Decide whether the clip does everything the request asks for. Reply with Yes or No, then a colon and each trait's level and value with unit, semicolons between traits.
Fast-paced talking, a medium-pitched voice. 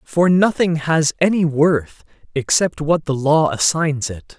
No: average, 150 wpm; medium, 155 Hz